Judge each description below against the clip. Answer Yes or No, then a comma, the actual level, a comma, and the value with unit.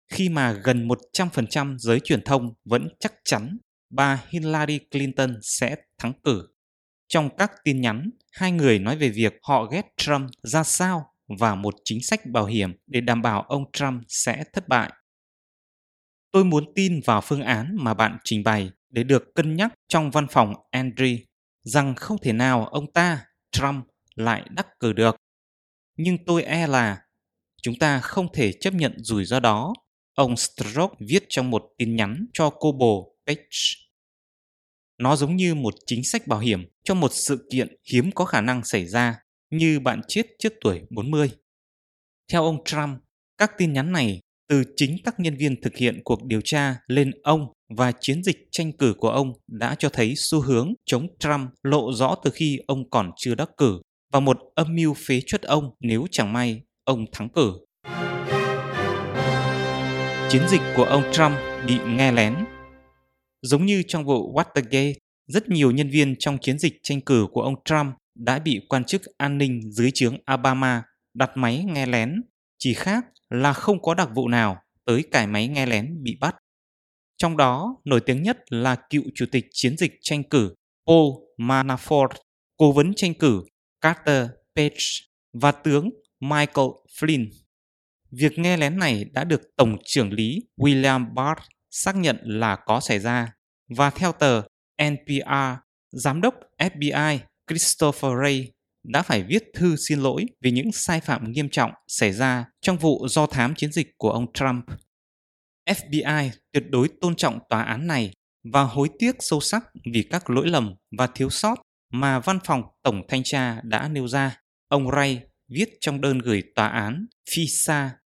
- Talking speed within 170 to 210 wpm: Yes, average, 175 wpm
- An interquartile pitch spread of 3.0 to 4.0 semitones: No, average, 4.4 semitones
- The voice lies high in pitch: No, low, 135 Hz